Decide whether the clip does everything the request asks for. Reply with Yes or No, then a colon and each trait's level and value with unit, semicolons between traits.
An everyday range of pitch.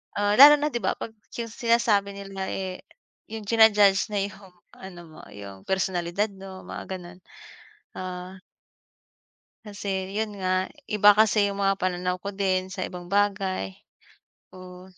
No: narrow, 2.0 semitones